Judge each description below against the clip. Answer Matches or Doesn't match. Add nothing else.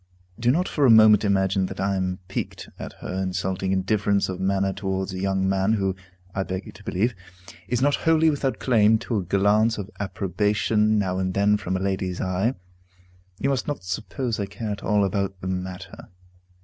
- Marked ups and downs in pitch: Doesn't match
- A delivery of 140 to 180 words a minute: Doesn't match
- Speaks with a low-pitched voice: Matches